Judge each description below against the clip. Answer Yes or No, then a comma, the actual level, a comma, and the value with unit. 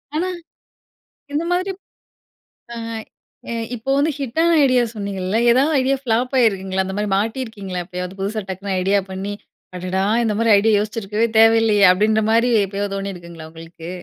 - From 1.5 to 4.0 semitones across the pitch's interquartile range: Yes, average, 3.7 semitones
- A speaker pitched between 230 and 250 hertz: No, high, 210 Hz